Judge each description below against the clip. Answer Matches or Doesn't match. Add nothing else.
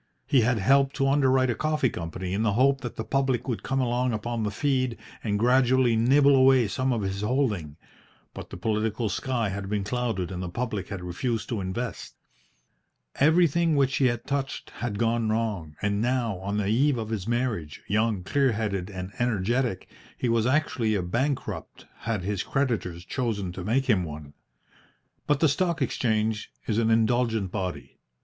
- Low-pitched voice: Matches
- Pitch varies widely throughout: Doesn't match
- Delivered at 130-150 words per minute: Doesn't match